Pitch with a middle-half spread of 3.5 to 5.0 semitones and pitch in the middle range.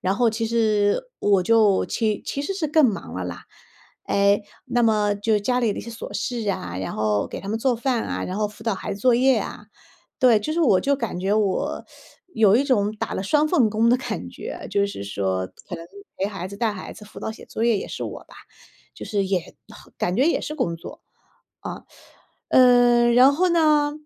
No: average, 3.9 semitones; high, 220 Hz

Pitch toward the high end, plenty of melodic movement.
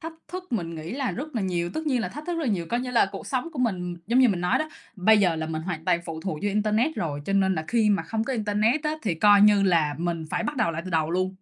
Yes: high, 205 Hz; wide, 6.1 semitones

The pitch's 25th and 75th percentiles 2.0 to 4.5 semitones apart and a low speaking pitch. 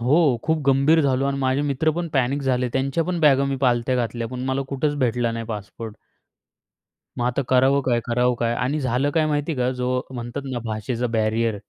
Yes: narrow, 2.6 semitones; low, 130 Hz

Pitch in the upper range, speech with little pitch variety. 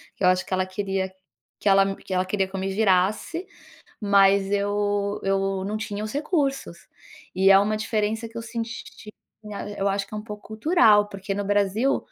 Yes: high, 205 Hz; narrow, 1.8 semitones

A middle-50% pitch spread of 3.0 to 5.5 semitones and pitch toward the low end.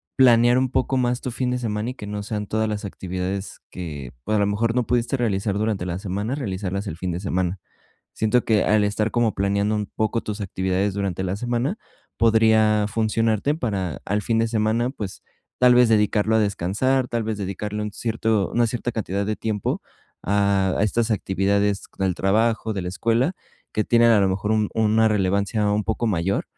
No: narrow, 2.6 semitones; low, 105 Hz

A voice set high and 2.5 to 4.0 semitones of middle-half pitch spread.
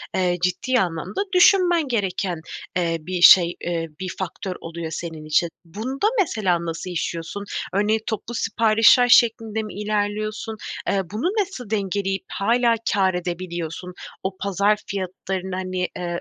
Yes: high, 195 Hz; average, 3.7 semitones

